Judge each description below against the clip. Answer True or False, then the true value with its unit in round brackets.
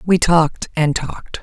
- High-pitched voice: False (160 Hz)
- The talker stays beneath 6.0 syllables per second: True (4.7 syllables/s)